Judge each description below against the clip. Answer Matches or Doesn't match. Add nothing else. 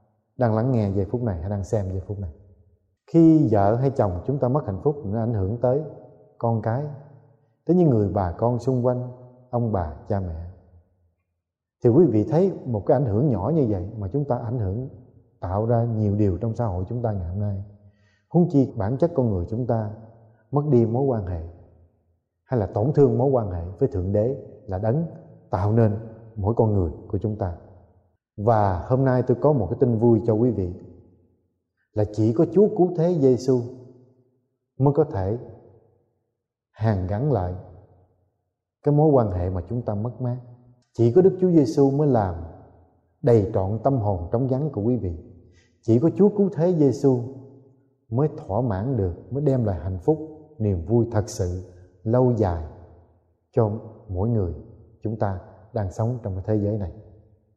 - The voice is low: Matches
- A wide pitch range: Doesn't match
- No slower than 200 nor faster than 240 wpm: Doesn't match